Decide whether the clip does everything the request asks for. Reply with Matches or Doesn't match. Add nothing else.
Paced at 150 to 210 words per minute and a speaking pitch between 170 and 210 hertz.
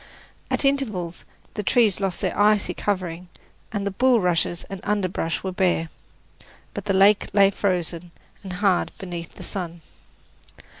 Doesn't match